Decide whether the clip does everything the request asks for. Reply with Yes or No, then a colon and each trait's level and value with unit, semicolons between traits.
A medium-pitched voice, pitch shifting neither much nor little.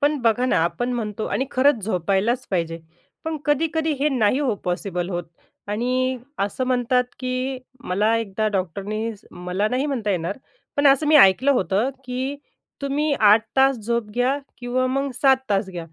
No: high, 245 Hz; average, 4.8 semitones